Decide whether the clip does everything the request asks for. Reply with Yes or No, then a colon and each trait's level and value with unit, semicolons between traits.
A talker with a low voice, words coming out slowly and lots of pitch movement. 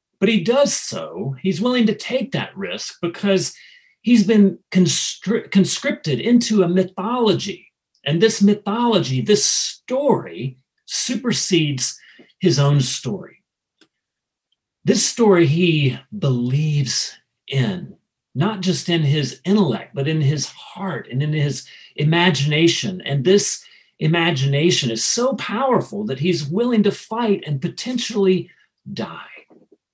No: medium, 185 Hz; slow, 120 wpm; wide, 6.3 semitones